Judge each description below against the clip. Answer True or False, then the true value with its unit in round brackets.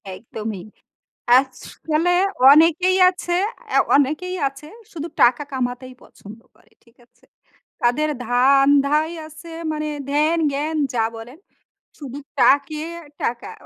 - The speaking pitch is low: False (285 Hz)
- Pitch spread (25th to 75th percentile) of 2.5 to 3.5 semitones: False (3.9 semitones)